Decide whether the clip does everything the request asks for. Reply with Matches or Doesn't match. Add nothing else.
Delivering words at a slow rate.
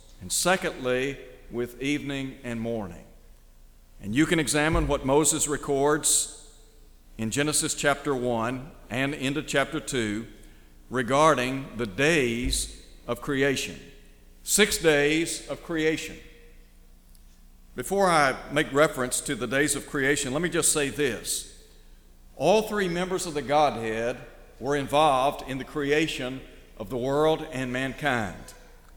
Matches